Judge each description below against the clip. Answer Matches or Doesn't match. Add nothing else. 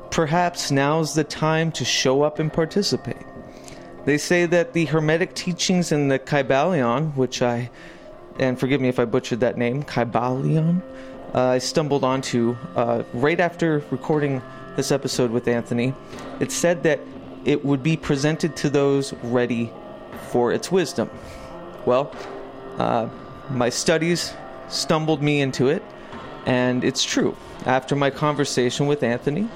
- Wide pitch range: Doesn't match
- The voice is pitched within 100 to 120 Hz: Doesn't match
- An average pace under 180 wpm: Matches